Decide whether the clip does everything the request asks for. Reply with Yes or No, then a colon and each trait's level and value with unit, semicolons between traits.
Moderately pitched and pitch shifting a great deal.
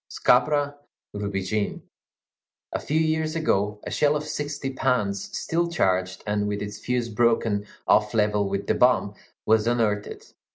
No: low, 110 Hz; wide, 5.9 semitones